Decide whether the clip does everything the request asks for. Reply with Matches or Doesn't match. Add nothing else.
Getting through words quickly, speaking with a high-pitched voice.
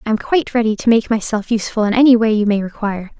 Matches